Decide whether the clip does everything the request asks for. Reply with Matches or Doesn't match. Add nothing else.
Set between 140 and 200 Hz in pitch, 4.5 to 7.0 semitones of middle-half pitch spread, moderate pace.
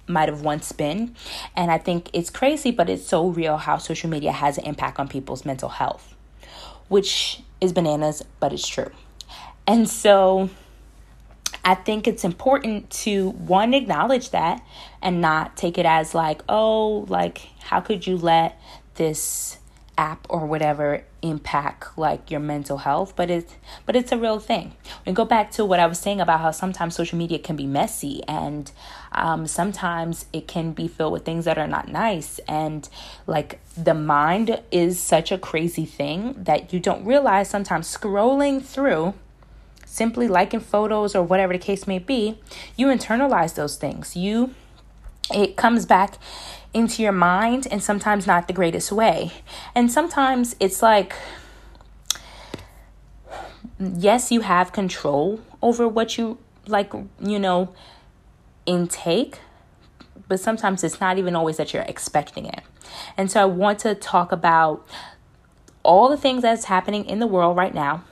Matches